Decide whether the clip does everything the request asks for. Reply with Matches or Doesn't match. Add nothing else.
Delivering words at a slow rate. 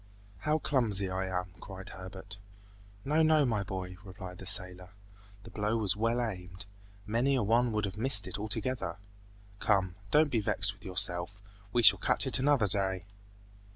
Doesn't match